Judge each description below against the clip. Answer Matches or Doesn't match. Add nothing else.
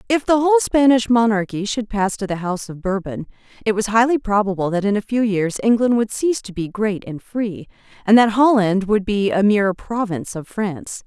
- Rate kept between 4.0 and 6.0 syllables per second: Matches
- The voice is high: Matches